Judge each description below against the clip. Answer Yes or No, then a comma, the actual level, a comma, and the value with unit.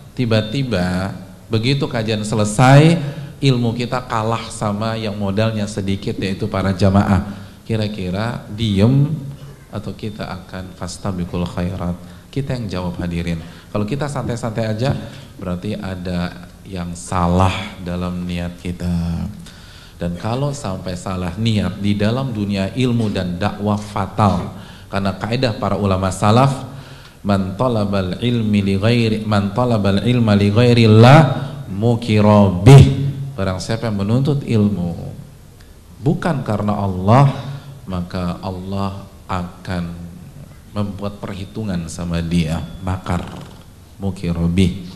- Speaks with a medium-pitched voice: No, low, 100 Hz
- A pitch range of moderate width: Yes, average, 4.0 semitones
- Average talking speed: Yes, average, 110 wpm